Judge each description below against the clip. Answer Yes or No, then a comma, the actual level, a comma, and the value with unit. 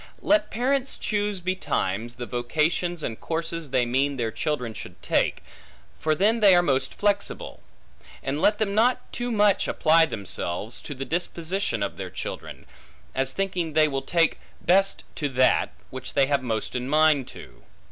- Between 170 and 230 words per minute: No, average, 160 wpm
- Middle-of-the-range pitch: Yes, medium, 155 Hz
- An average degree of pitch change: No, wide, 7.0 semitones